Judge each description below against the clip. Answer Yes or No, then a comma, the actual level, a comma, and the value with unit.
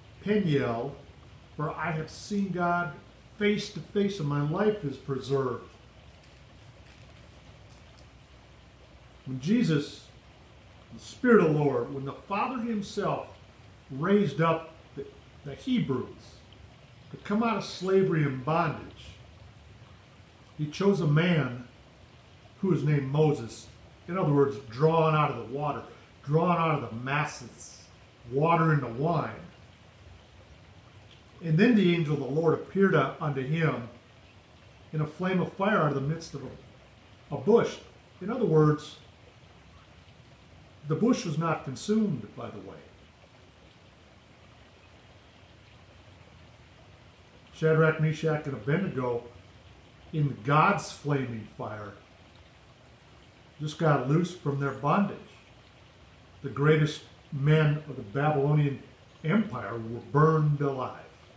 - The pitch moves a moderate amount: No, wide, 6.3 semitones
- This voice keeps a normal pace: No, slow, 115 wpm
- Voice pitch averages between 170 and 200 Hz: No, medium, 140 Hz